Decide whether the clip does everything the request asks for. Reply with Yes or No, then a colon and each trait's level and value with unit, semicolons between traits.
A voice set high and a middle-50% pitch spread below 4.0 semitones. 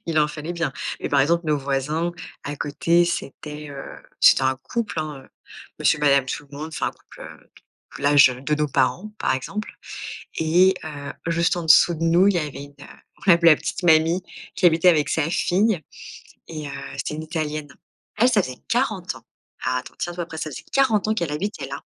No: medium, 155 Hz; average, 3.2 semitones